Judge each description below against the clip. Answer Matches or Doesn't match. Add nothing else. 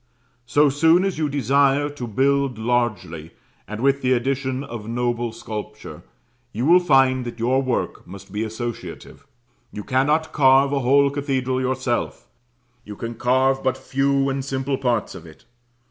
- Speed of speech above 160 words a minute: Doesn't match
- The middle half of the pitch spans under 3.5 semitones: Matches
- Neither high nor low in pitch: Doesn't match